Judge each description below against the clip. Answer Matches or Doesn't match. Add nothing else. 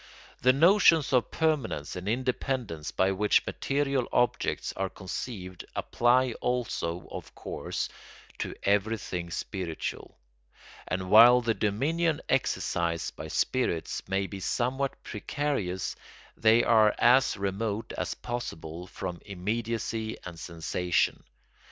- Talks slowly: Matches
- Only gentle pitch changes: Doesn't match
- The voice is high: Doesn't match